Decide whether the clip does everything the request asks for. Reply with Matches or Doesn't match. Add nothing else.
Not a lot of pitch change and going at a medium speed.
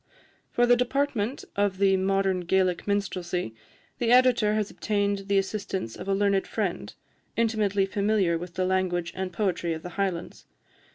Matches